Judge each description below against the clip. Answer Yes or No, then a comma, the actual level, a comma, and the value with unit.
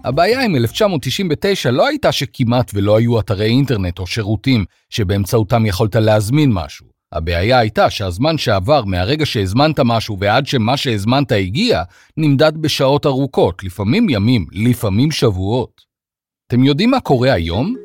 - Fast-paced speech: No, average, 130 wpm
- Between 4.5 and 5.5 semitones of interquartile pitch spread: Yes, average, 5.0 semitones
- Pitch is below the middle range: Yes, low, 120 Hz